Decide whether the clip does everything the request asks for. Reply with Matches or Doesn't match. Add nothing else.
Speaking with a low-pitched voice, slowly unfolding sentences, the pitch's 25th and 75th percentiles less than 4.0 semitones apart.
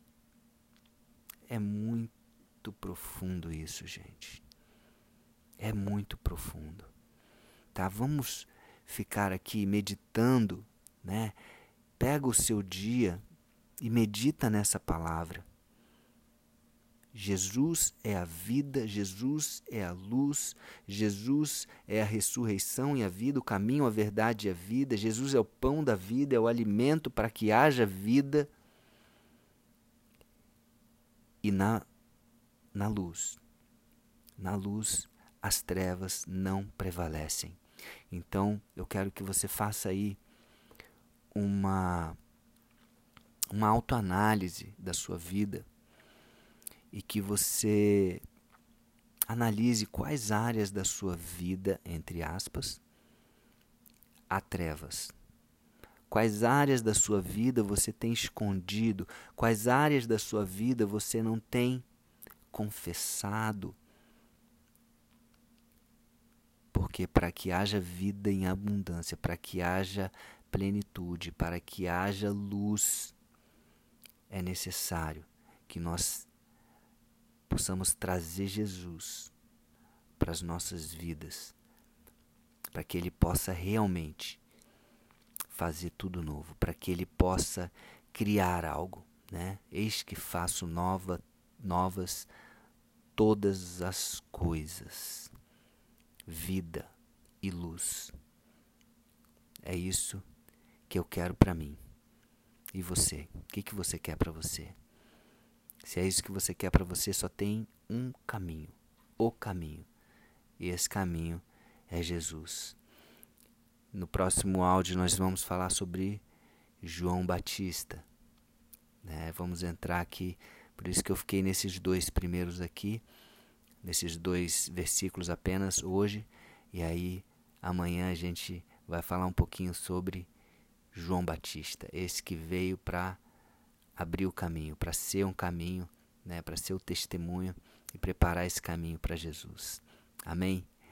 Matches